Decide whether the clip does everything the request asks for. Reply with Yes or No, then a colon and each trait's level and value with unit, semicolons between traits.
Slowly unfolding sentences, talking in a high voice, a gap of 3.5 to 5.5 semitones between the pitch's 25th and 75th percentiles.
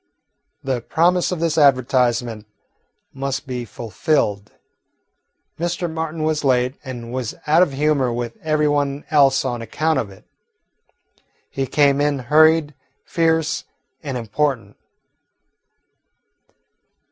No: slow, 110 wpm; medium, 140 Hz; average, 3.9 semitones